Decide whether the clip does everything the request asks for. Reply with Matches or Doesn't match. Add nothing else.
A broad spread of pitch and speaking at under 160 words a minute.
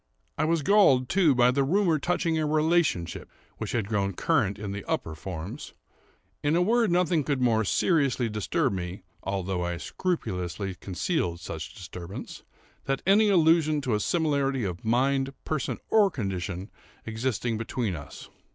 Matches